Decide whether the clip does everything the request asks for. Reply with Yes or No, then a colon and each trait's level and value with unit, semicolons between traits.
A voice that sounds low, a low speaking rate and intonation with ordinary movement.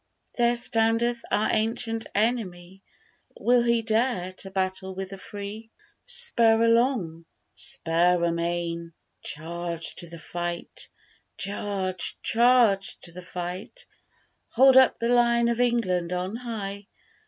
No: high, 200 Hz; slow, 120 wpm; average, 4.9 semitones